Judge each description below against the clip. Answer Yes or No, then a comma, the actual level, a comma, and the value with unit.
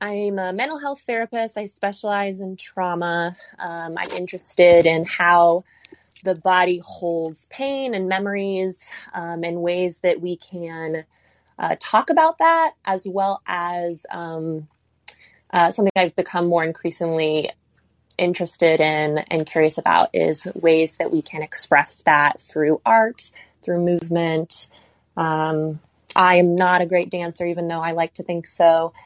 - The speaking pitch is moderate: Yes, medium, 175 Hz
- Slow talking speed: No, average, 145 wpm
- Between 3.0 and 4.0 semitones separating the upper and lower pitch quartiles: No, narrow, 2.4 semitones